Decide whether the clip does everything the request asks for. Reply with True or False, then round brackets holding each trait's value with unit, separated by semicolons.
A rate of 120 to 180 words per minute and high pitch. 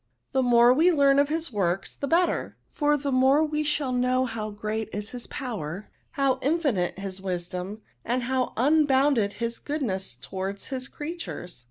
True (165 wpm; 250 Hz)